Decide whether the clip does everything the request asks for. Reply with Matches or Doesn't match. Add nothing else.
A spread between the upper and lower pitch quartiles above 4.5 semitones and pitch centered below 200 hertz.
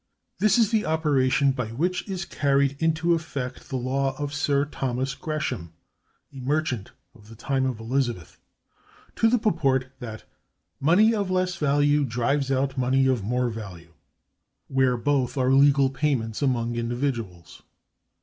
Doesn't match